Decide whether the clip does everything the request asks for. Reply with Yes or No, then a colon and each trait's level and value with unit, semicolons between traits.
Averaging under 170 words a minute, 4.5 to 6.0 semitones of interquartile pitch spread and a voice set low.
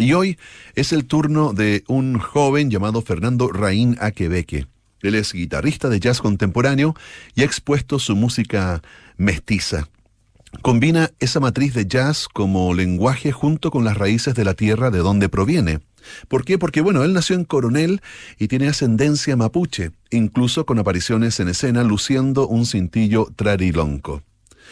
Yes: average, 150 wpm; wide, 5.5 semitones; low, 115 Hz